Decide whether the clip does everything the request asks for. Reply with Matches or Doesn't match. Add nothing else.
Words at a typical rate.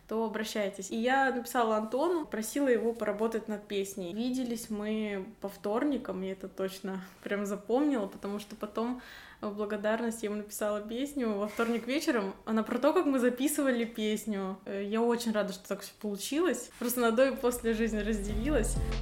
Doesn't match